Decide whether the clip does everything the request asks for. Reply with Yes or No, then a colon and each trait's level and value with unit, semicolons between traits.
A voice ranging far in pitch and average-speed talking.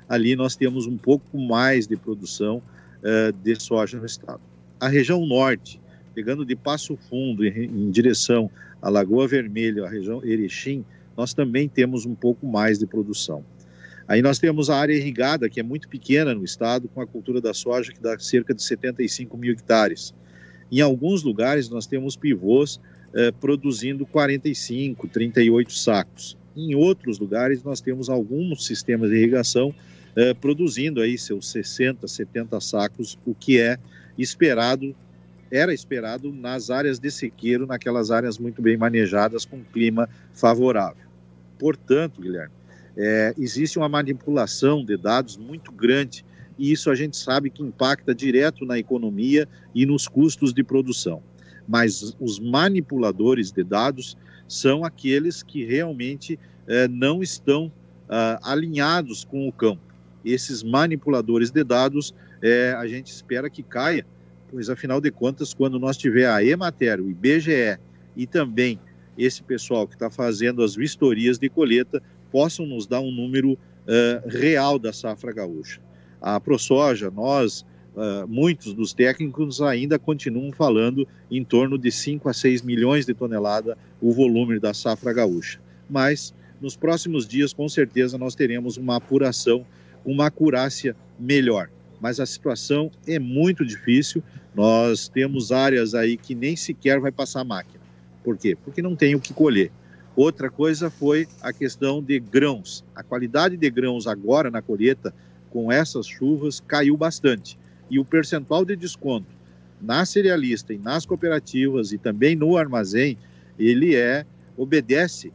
No: average, 4.2 semitones; average, 150 wpm